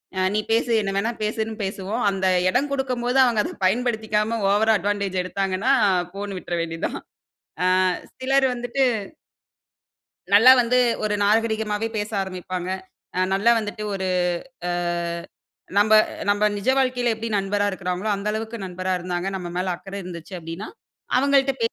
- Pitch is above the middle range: Yes, high, 210 Hz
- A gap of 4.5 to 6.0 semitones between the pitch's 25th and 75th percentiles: No, average, 3.6 semitones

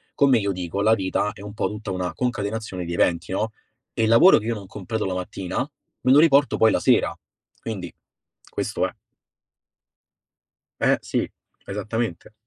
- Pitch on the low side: Yes, low, 105 Hz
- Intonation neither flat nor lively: Yes, average, 3.3 semitones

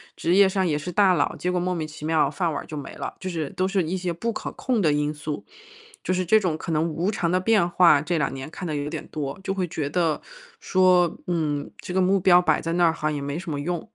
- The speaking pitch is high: No, medium, 170 Hz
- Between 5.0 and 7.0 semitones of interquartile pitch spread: No, average, 3.2 semitones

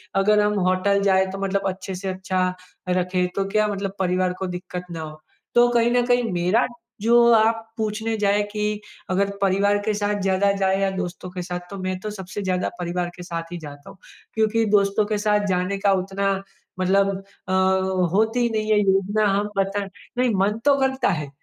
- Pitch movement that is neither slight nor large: No, narrow, 2.3 semitones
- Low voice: No, high, 195 Hz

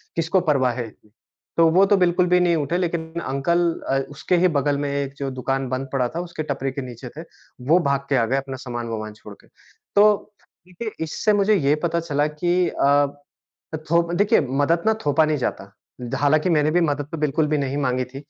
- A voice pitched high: No, medium, 145 Hz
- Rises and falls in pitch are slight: No, average, 4.1 semitones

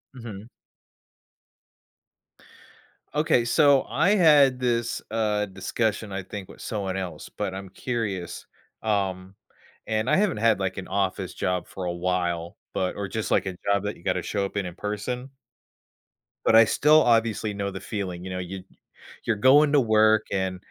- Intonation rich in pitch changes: No, average, 3.6 semitones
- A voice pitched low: Yes, low, 105 Hz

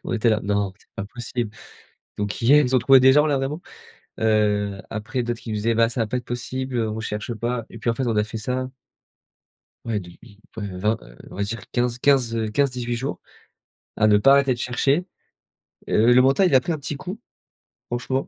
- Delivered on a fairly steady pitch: No, average, 3.5 semitones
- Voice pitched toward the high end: No, low, 120 Hz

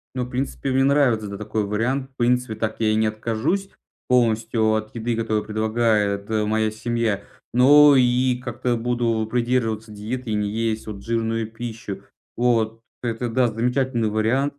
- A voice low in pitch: Yes, low, 115 Hz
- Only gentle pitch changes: Yes, narrow, 2.3 semitones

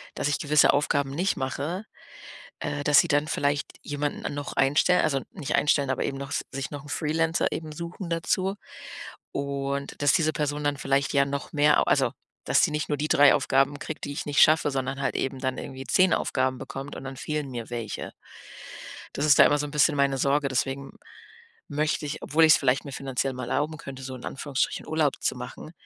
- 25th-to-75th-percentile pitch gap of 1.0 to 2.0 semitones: Yes, narrow, 1.7 semitones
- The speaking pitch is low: No, medium, 145 Hz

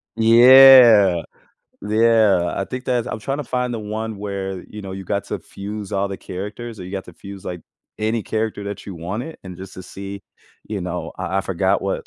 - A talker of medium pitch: No, low, 100 Hz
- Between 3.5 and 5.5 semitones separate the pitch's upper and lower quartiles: No, average, 2.8 semitones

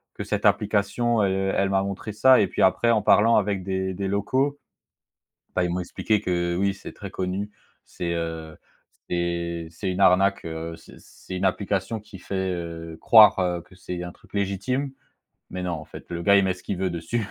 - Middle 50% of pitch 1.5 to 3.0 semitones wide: Yes, narrow, 2.6 semitones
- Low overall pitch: Yes, very low, 95 Hz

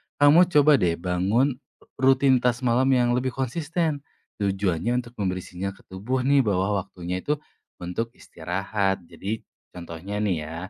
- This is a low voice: Yes, low, 110 Hz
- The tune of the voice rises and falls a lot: Yes, wide, 6.0 semitones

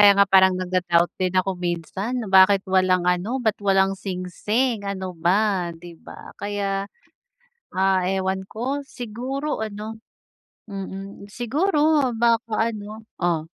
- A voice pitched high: Yes, high, 195 Hz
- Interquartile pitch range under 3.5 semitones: Yes, average, 3.0 semitones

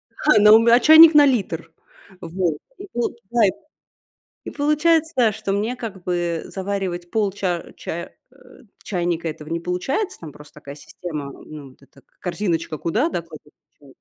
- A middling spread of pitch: No, wide, 6.0 semitones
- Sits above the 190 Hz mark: No, medium, 185 Hz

